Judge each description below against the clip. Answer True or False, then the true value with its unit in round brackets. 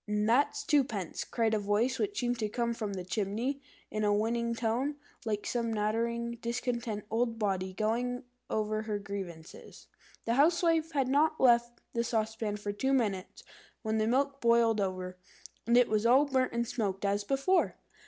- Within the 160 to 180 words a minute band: True (170 wpm)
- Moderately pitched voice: False (230 Hz)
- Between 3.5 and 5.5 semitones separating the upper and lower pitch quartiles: False (2.9 semitones)